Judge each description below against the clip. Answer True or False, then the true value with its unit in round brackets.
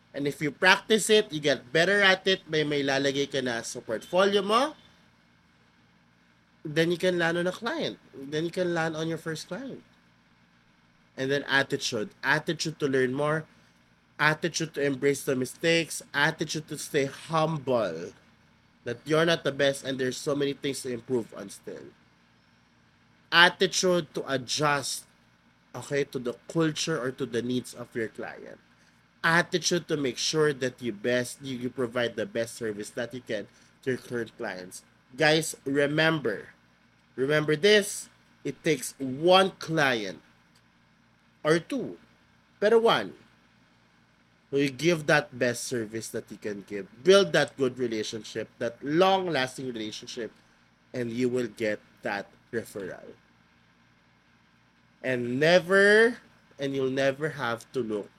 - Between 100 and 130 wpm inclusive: False (145 wpm)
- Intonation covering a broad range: True (6.8 semitones)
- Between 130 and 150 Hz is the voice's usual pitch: True (135 Hz)